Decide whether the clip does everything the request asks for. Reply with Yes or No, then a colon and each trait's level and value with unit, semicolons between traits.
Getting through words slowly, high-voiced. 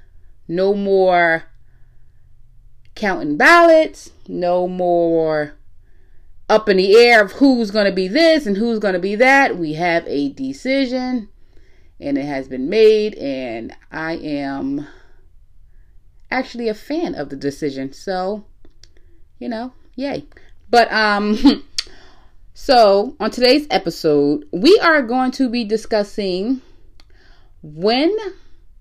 Yes: slow, 120 wpm; high, 205 Hz